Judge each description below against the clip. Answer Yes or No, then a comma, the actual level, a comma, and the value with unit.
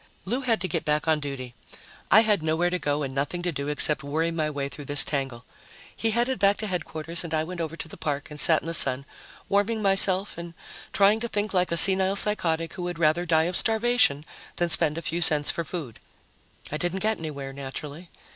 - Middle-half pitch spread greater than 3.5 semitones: Yes, average, 4.3 semitones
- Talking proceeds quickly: Yes, fast, 220 wpm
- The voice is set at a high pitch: No, medium, 165 Hz